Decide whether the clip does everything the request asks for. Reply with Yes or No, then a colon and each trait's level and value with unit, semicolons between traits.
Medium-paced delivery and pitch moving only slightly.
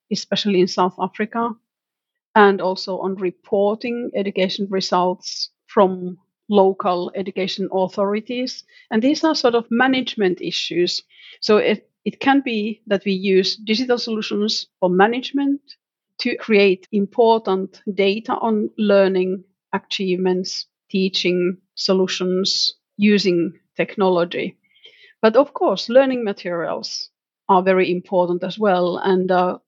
No: average, 115 wpm; average, 3.3 semitones